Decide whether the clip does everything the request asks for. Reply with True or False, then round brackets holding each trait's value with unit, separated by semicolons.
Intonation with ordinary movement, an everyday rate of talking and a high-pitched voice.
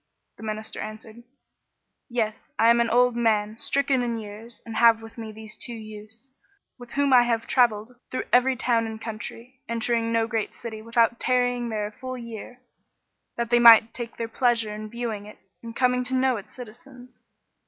False (2.0 semitones; 185 wpm; 230 Hz)